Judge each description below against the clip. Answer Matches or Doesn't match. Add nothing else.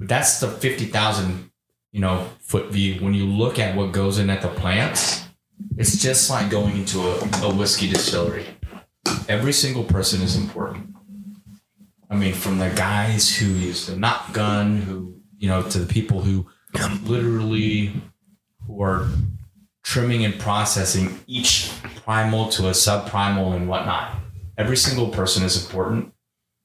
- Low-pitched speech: Matches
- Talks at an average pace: Matches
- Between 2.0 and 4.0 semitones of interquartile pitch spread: Matches